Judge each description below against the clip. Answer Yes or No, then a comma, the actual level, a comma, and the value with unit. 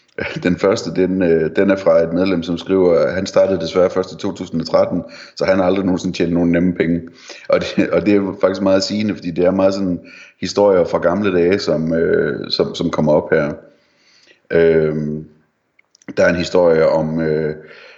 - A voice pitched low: Yes, very low, 90 Hz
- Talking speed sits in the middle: Yes, average, 180 wpm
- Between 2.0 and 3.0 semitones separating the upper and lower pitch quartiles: Yes, average, 2.7 semitones